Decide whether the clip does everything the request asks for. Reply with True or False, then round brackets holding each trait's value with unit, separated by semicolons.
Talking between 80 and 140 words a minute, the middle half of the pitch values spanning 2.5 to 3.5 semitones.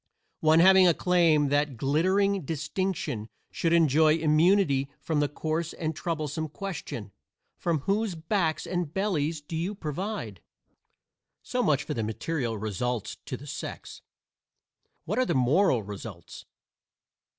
False (135 wpm; 4.3 semitones)